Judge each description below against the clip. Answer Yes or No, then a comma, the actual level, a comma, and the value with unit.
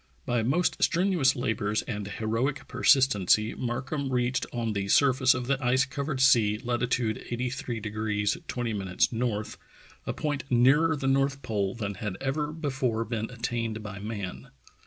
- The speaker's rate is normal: Yes, average, 150 wpm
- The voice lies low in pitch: Yes, low, 120 Hz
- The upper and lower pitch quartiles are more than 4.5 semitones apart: No, average, 3.8 semitones